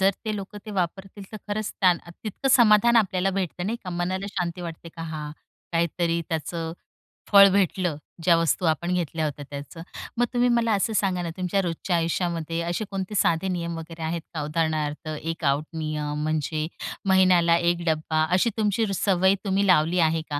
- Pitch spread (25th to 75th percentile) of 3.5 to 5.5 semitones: No, average, 3.1 semitones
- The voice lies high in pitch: No, medium, 175 Hz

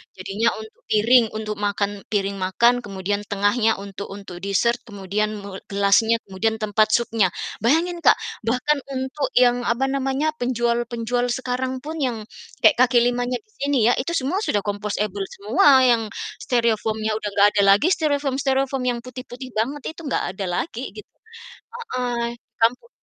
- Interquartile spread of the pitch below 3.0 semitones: No, average, 4.0 semitones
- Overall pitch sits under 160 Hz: No, high, 235 Hz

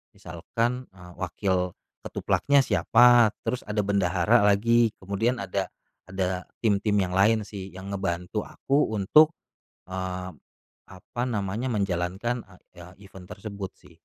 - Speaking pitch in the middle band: No, low, 100 Hz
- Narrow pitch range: No, average, 3.6 semitones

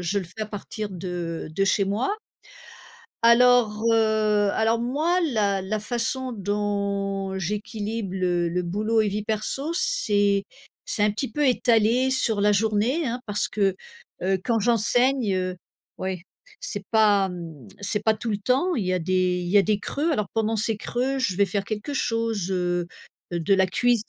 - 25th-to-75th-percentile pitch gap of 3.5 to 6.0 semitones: No, average, 3.1 semitones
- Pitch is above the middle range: Yes, high, 210 Hz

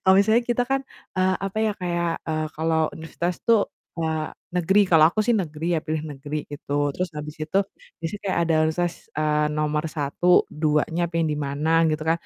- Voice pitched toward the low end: No, medium, 165 Hz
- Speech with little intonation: No, average, 3.1 semitones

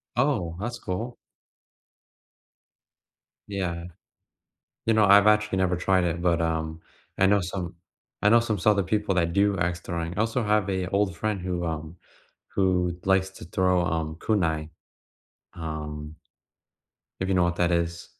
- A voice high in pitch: No, very low, 90 Hz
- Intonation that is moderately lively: Yes, average, 3.3 semitones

